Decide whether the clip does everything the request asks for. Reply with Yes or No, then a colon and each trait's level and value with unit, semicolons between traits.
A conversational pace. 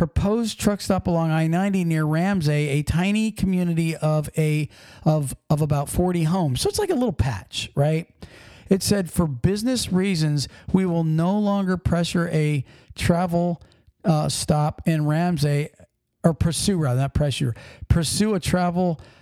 Yes: average, 150 wpm